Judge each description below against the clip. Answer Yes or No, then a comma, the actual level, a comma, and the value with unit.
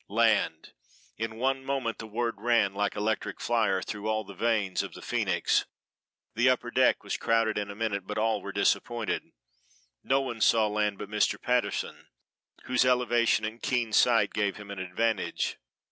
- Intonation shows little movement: Yes, narrow, 2.3 semitones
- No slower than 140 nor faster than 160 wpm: No, average, 170 wpm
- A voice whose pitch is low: Yes, low, 110 Hz